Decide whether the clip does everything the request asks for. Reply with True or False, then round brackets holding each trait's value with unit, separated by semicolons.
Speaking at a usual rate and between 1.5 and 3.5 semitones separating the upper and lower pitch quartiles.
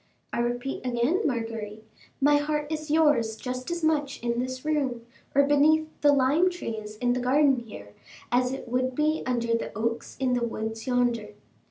False (175 wpm; 3.9 semitones)